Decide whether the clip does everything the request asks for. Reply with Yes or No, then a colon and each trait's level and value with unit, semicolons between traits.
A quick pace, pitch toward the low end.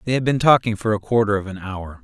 Yes: fast, 295 wpm; low, 110 Hz